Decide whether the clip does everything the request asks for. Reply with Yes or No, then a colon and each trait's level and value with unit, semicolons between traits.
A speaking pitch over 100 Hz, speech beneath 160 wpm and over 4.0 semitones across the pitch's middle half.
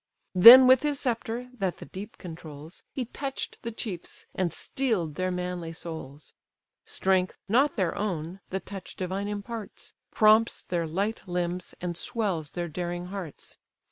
Yes: medium, 185 Hz; average, 145 wpm; average, 4.5 semitones